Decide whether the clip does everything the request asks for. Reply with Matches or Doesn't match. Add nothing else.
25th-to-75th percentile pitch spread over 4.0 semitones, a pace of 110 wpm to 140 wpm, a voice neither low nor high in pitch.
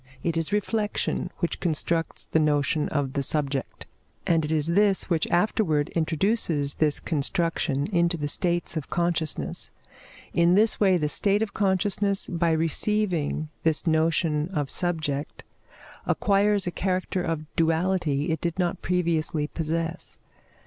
Doesn't match